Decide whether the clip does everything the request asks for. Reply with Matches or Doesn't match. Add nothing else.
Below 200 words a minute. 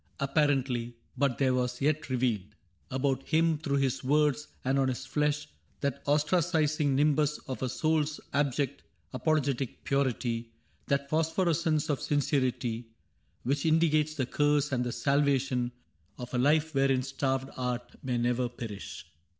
Matches